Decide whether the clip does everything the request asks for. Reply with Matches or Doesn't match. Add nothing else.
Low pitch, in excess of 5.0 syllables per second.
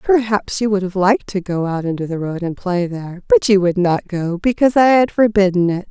Doesn't match